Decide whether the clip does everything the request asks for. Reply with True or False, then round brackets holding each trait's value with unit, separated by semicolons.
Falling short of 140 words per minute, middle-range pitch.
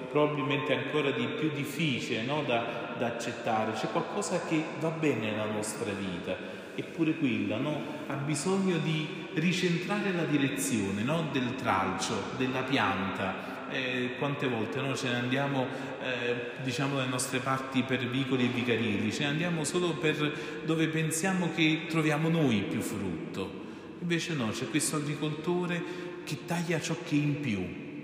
False (150 wpm; 145 Hz)